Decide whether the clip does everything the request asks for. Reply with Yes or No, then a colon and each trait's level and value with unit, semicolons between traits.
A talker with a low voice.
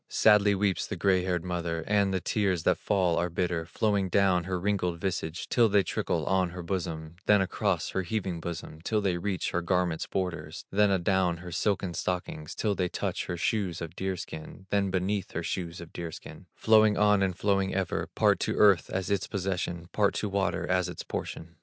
Yes: very low, 95 Hz